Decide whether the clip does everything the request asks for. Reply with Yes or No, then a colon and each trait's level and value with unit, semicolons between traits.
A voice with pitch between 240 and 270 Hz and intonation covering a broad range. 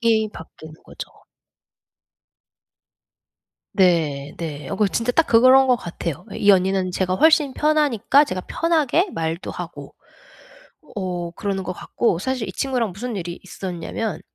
No: high, 200 Hz; wide, 6.4 semitones